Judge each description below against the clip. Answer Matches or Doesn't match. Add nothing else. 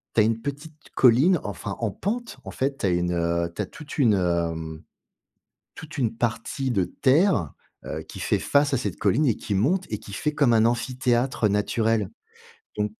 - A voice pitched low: Matches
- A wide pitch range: Matches